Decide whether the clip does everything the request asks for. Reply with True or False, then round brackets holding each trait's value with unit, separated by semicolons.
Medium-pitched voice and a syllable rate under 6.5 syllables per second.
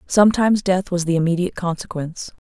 False (180 Hz; 6.8 syllables/s)